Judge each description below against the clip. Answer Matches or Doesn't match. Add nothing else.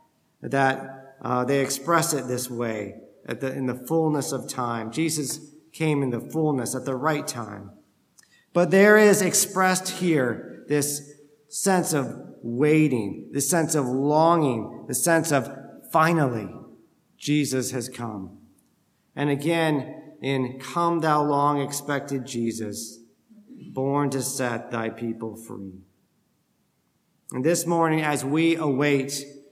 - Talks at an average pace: Doesn't match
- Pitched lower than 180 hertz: Matches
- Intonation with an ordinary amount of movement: Matches